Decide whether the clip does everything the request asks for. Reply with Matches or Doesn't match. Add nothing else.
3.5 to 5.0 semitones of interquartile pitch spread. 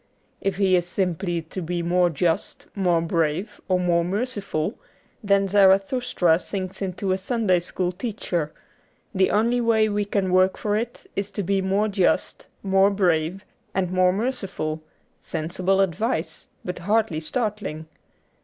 Doesn't match